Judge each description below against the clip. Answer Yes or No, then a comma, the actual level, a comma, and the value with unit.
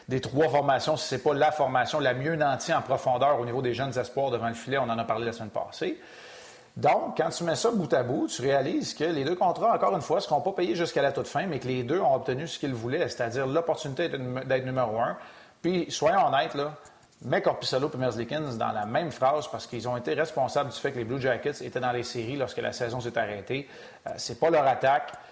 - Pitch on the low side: Yes, low, 130 Hz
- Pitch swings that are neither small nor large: Yes, average, 3.7 semitones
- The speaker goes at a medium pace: No, fast, 245 wpm